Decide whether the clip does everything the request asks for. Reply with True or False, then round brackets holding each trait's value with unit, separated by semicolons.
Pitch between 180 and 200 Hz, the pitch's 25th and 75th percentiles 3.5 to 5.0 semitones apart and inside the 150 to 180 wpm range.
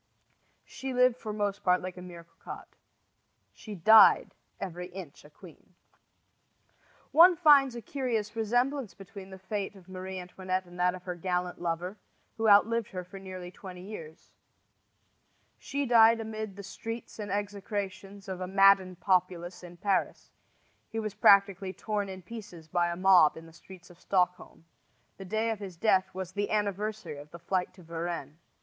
False (190 Hz; 3.0 semitones; 165 wpm)